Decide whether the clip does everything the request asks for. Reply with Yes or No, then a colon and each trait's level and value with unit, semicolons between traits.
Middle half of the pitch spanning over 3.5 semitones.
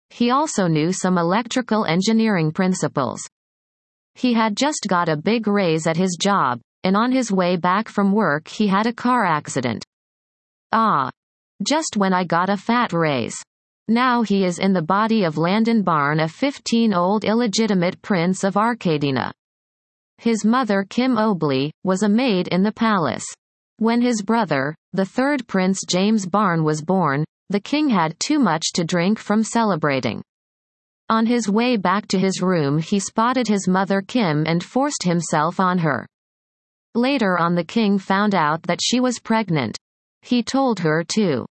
Yes: average, 4.6 semitones